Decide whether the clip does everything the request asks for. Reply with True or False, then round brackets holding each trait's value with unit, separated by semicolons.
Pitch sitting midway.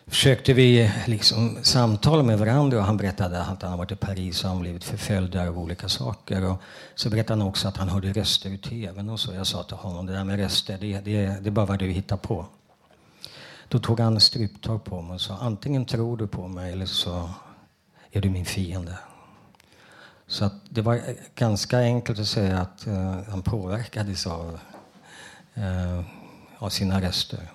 False (100 Hz)